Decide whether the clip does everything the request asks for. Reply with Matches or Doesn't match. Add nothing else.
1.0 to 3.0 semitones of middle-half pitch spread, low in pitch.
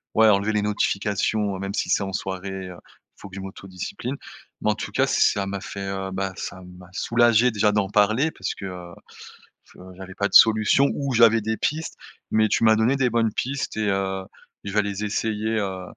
Matches